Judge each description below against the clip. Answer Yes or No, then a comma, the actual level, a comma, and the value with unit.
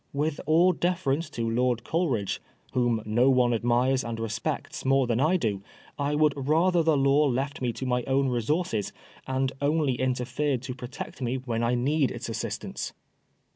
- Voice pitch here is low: Yes, low, 130 Hz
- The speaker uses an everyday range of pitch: Yes, average, 3.5 semitones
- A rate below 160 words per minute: No, average, 170 wpm